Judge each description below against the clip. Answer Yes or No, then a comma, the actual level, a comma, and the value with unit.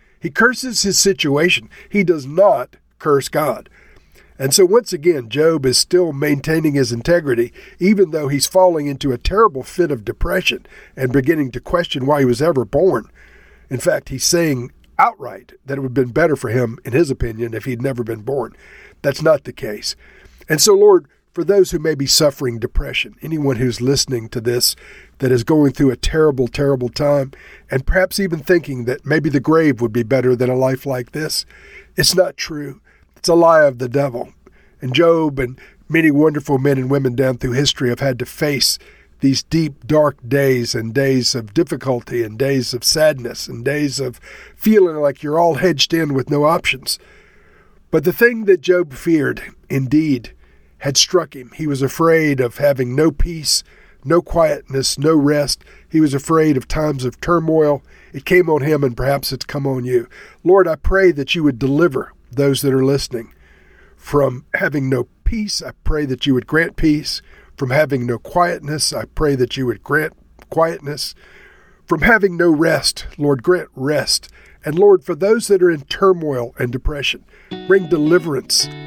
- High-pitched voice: No, medium, 145 Hz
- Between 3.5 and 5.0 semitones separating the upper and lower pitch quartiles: Yes, average, 4.3 semitones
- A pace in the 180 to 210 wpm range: Yes, average, 185 wpm